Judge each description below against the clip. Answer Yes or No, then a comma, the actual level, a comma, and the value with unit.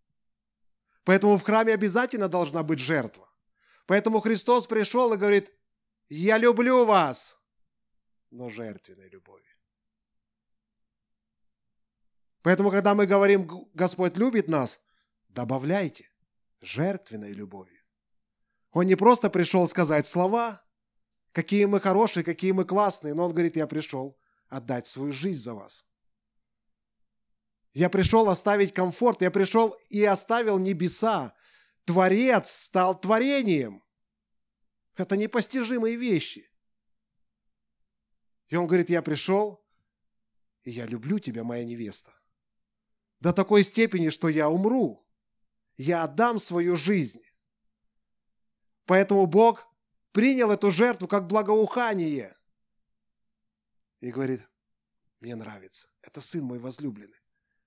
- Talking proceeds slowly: Yes, slow, 105 wpm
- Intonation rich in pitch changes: Yes, wide, 8.4 semitones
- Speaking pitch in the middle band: Yes, medium, 180 Hz